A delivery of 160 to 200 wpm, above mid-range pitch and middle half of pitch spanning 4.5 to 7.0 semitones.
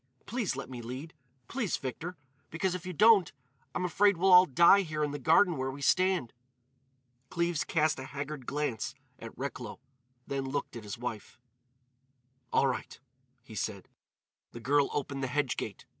No: average, 165 wpm; medium, 145 Hz; wide, 5.4 semitones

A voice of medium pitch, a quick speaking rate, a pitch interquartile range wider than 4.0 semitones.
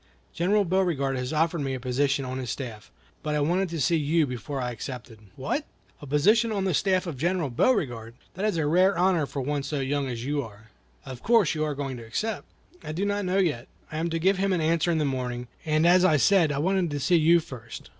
Yes: medium, 150 Hz; fast, 235 wpm; wide, 5.4 semitones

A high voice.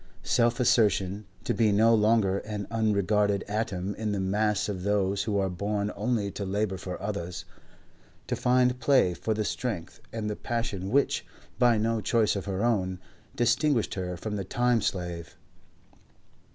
No: low, 105 Hz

